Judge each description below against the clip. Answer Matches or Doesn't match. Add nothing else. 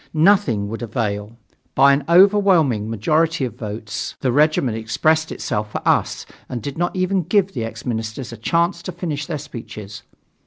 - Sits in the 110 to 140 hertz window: Matches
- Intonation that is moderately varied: Doesn't match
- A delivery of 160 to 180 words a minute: Matches